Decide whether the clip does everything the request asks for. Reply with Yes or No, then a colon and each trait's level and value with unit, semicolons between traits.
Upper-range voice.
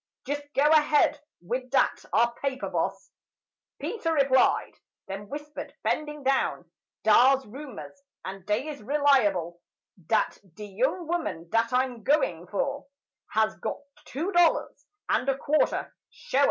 Yes: very high, 270 Hz